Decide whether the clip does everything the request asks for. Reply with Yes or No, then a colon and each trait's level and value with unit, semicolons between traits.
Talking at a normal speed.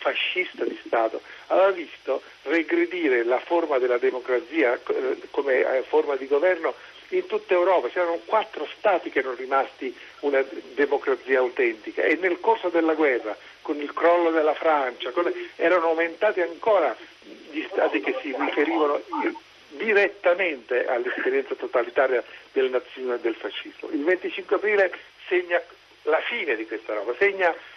Yes: average, 135 wpm